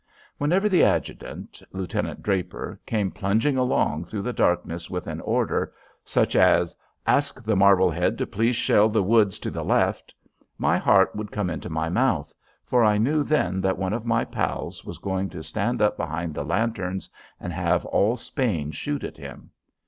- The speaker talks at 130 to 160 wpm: No, average, 175 wpm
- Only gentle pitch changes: No, average, 4.6 semitones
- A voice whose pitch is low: Yes, low, 100 Hz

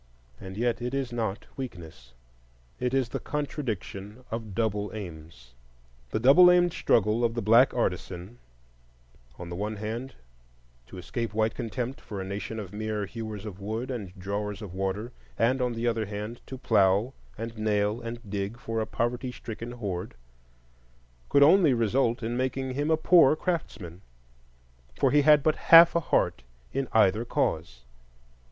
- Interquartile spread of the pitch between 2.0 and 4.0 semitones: No, average, 4.7 semitones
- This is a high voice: No, low, 110 Hz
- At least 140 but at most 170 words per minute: Yes, average, 155 wpm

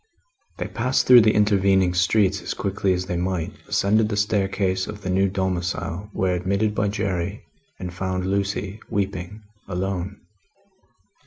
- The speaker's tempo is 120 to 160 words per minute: Yes, average, 145 wpm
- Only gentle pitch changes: Yes, narrow, 2.0 semitones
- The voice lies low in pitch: Yes, very low, 95 Hz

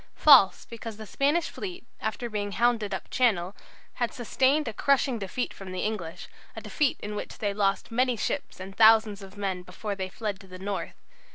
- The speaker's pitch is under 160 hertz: No, high, 215 Hz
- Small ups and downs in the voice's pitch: No, average, 3.7 semitones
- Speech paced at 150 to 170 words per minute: No, average, 190 wpm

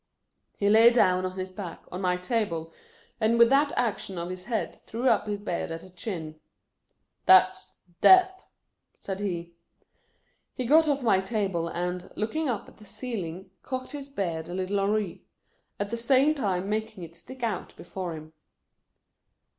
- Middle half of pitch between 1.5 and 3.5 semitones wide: No, average, 4.5 semitones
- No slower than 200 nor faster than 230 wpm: No, average, 175 wpm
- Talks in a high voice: Yes, high, 200 Hz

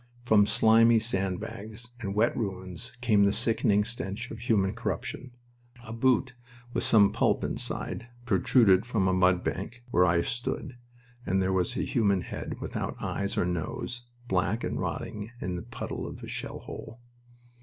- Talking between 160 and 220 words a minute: Yes, average, 165 wpm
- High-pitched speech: No, low, 105 Hz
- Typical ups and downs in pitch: Yes, average, 3.6 semitones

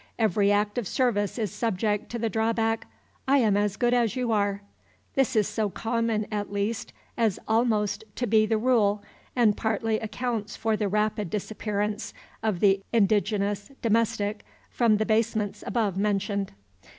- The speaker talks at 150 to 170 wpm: Yes, average, 155 wpm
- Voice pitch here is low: No, high, 215 Hz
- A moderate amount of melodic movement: No, narrow, 1.9 semitones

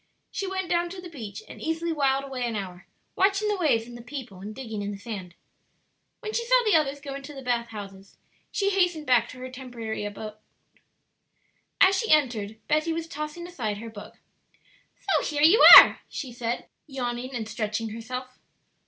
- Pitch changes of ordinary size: No, wide, 6.5 semitones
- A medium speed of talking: Yes, average, 190 wpm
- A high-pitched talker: Yes, very high, 255 Hz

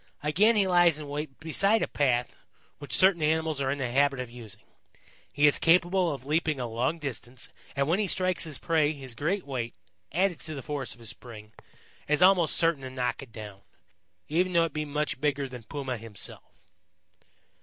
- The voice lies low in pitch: No, medium, 145 Hz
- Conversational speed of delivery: Yes, average, 195 wpm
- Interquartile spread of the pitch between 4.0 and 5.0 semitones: Yes, average, 4.5 semitones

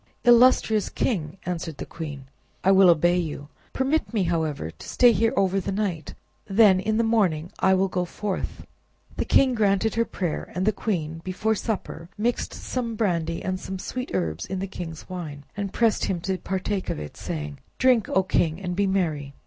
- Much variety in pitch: No, average, 4.5 semitones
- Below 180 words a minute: No, average, 190 wpm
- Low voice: No, high, 190 Hz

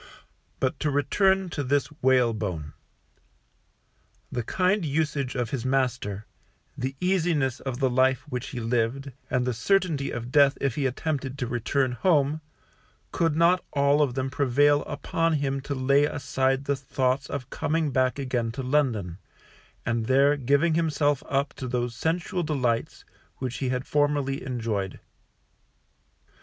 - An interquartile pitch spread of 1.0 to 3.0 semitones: Yes, narrow, 2.6 semitones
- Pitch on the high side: No, low, 135 Hz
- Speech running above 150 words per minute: No, average, 145 wpm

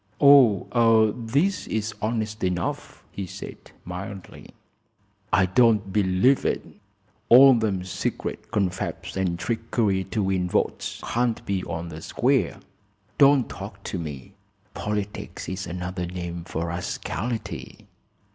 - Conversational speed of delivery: No, slow, 120 wpm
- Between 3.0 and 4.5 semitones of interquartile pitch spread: Yes, average, 4.0 semitones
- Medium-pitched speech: No, low, 100 Hz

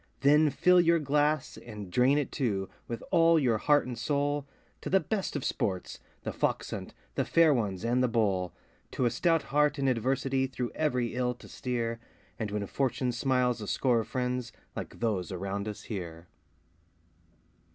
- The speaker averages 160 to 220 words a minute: Yes, average, 175 wpm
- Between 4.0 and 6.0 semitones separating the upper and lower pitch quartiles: Yes, average, 4.4 semitones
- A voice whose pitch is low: Yes, low, 125 Hz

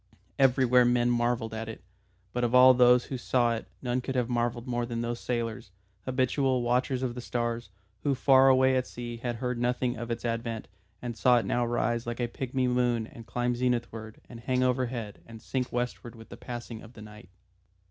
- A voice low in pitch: Yes, low, 120 Hz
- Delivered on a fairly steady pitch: Yes, narrow, 1.3 semitones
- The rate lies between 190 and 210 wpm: Yes, average, 200 wpm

